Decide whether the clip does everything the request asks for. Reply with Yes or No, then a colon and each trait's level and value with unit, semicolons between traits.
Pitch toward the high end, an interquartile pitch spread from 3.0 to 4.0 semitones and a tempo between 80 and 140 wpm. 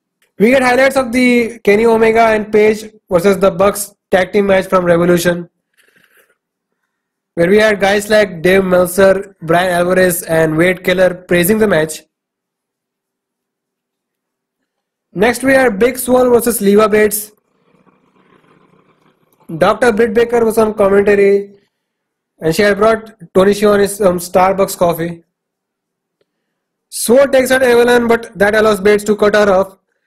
Yes: high, 205 Hz; average, 3.3 semitones; slow, 135 wpm